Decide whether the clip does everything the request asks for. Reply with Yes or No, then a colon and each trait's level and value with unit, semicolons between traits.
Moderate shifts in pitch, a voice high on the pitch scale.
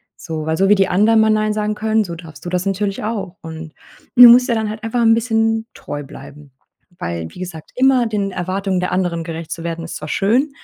Yes: average, 4.9 semitones; high, 195 Hz